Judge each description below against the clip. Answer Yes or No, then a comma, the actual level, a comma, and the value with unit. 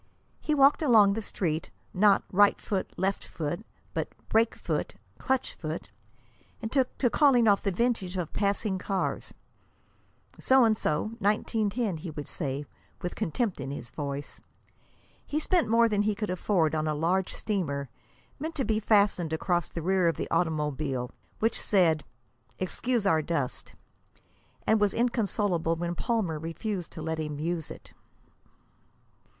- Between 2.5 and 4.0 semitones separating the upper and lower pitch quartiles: No, wide, 5.4 semitones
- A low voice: No, high, 190 Hz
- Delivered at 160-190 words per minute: No, average, 150 wpm